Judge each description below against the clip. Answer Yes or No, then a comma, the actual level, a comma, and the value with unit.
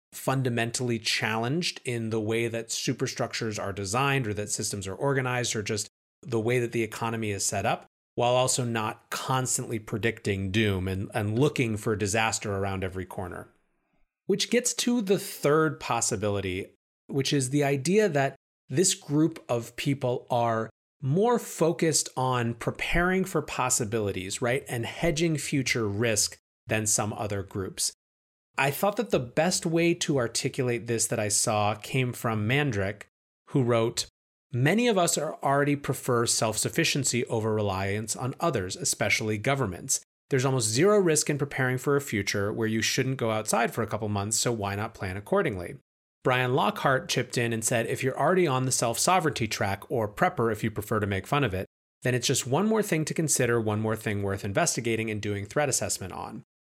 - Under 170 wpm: No, average, 175 wpm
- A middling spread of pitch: Yes, average, 4.6 semitones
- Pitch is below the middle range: Yes, low, 120 Hz